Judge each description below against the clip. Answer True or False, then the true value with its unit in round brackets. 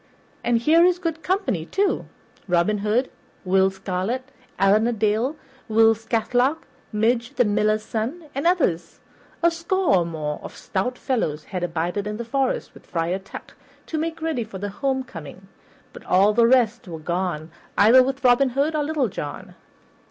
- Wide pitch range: True (5.8 semitones)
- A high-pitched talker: True (225 Hz)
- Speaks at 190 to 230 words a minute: False (165 wpm)